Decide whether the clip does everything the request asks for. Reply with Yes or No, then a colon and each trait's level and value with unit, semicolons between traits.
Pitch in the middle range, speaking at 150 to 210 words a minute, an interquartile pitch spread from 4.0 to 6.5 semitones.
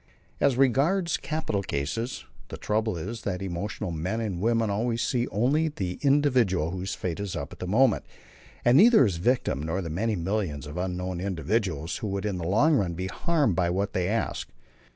No: low, 100 Hz; average, 190 wpm; average, 5.1 semitones